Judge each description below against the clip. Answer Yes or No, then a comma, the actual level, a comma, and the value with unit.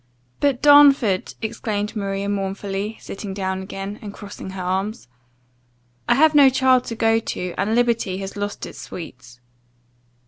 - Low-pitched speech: No, high, 205 Hz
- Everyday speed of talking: Yes, average, 145 wpm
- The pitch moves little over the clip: No, average, 3.2 semitones